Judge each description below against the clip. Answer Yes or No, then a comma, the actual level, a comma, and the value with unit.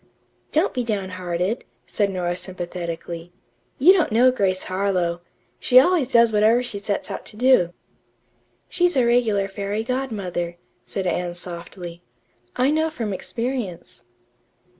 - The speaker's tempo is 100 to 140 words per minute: Yes, slow, 135 wpm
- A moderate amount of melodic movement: No, wide, 5.8 semitones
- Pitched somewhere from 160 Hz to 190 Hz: No, high, 200 Hz